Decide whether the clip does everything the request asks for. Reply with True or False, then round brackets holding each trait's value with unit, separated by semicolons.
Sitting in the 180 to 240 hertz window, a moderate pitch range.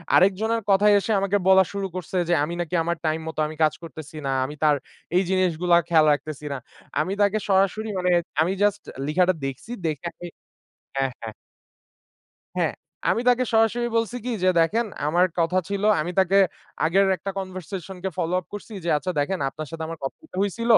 True (185 Hz; 3.7 semitones)